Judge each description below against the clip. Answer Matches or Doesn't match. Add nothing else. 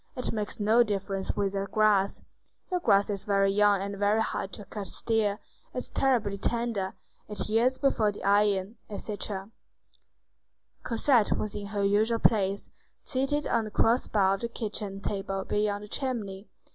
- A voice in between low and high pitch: Doesn't match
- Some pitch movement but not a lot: Doesn't match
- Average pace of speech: Matches